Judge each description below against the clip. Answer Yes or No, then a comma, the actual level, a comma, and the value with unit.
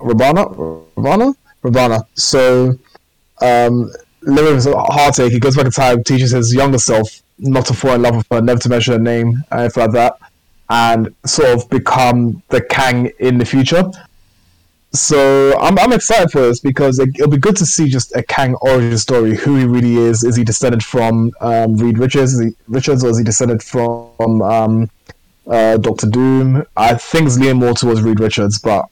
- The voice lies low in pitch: Yes, low, 120 Hz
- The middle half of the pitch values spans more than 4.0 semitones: No, average, 2.7 semitones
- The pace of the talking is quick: No, average, 190 wpm